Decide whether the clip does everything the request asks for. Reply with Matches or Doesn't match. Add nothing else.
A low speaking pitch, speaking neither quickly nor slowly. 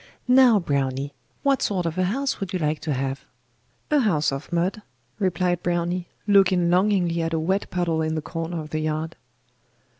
Doesn't match